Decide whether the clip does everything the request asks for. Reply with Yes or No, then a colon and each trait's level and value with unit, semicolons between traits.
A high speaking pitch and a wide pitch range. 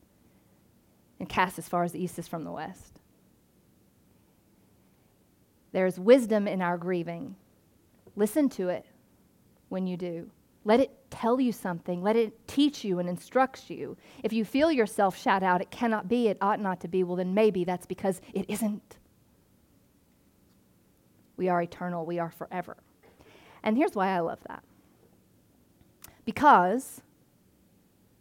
No: high, 195 Hz; average, 3.9 semitones